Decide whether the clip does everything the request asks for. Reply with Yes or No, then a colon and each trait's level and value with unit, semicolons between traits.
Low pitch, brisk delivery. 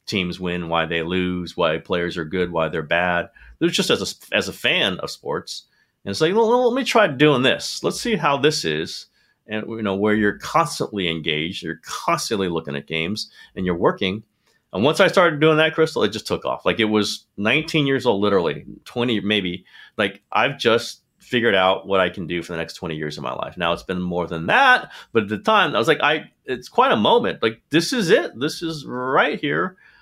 Yes: low, 105 Hz; fast, 225 wpm